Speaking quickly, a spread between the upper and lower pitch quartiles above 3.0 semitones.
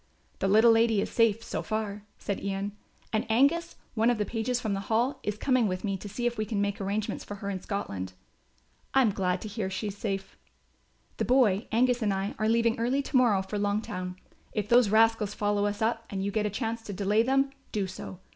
No: fast, 225 wpm; narrow, 2.5 semitones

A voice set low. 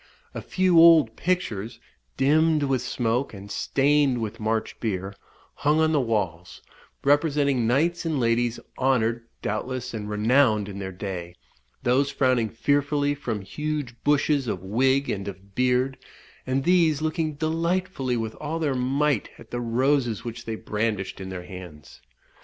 Yes: low, 125 Hz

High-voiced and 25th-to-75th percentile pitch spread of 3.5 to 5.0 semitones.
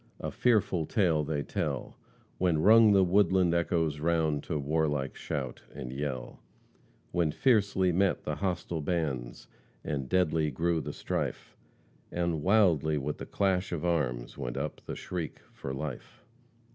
No: very low, 80 Hz; average, 3.8 semitones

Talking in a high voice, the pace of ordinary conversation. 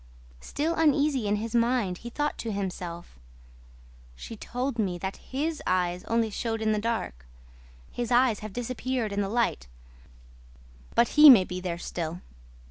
Yes: high, 225 Hz; average, 155 wpm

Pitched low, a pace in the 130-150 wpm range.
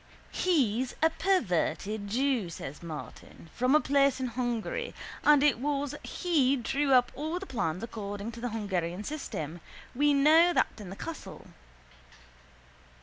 No: very high, 255 Hz; average, 145 wpm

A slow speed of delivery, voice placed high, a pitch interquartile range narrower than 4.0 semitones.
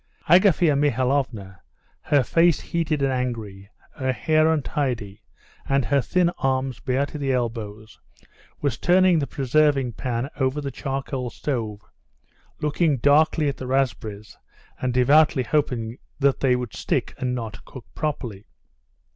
No: slow, 130 wpm; low, 135 Hz; average, 3.5 semitones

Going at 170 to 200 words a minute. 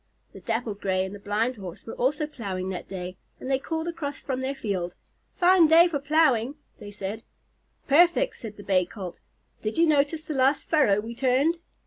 Yes: average, 190 wpm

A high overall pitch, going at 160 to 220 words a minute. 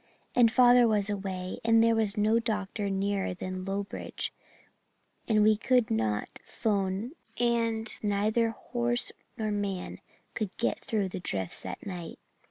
No: high, 210 Hz; average, 140 wpm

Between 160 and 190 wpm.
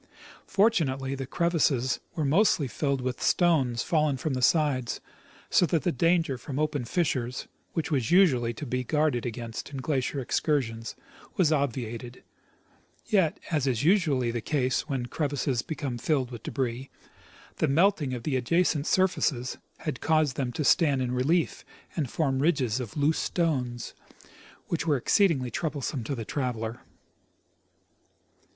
No: average, 145 wpm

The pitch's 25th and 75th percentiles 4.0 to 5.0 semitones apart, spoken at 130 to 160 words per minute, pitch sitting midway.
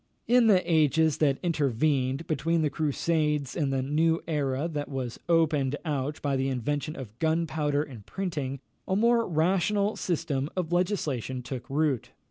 No: average, 3.5 semitones; average, 150 wpm; medium, 150 Hz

